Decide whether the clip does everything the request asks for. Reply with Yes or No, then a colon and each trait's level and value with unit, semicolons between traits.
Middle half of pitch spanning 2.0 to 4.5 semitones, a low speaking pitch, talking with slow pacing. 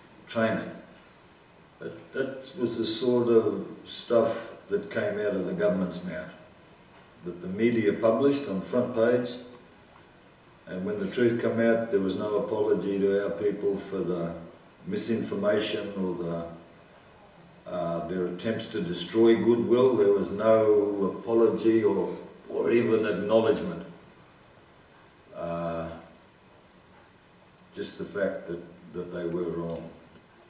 No: average, 5.0 semitones; low, 100 Hz; slow, 125 wpm